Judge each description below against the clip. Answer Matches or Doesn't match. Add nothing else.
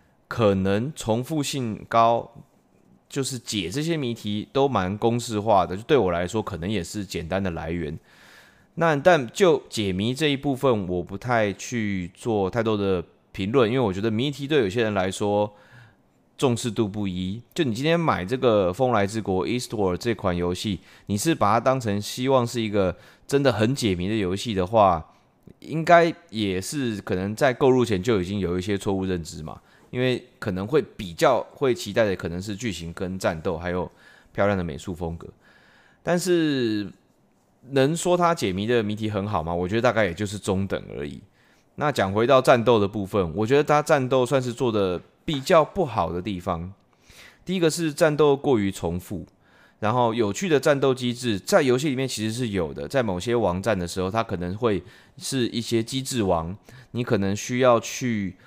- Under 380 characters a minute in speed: Matches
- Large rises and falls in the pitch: Doesn't match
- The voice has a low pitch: Matches